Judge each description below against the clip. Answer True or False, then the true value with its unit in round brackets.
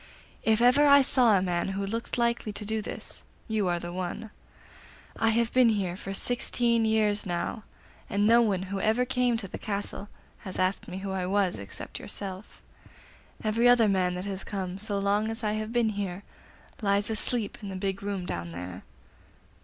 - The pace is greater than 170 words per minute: True (190 wpm)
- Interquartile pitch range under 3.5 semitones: True (3.0 semitones)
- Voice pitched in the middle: False (205 Hz)